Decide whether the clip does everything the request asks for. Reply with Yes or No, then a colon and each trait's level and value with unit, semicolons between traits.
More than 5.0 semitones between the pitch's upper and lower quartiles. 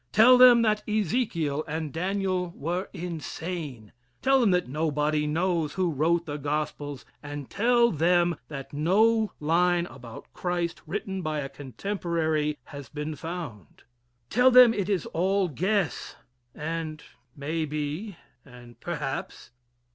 No: average, 4.3 semitones